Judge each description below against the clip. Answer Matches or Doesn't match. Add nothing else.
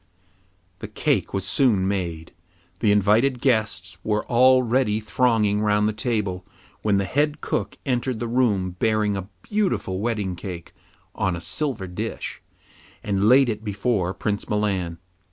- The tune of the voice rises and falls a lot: Doesn't match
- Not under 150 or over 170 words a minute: Doesn't match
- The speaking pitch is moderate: Doesn't match